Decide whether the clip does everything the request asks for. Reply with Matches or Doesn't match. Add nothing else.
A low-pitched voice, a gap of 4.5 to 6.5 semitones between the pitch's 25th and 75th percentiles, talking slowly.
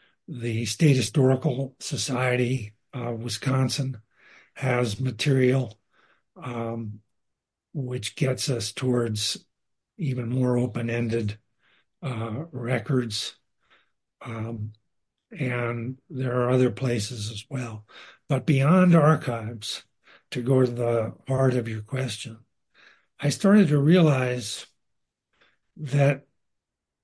Doesn't match